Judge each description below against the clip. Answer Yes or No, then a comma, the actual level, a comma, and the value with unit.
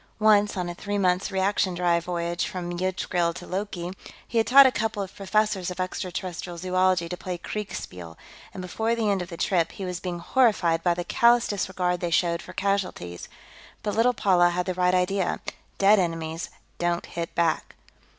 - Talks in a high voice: No, medium, 180 Hz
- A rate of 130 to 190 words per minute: Yes, average, 185 wpm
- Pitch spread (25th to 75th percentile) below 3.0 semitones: Yes, narrow, 2.5 semitones